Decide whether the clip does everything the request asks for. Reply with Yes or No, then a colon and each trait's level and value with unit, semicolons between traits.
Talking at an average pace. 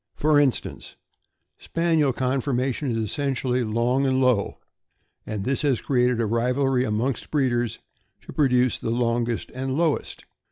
Yes: average, 145 wpm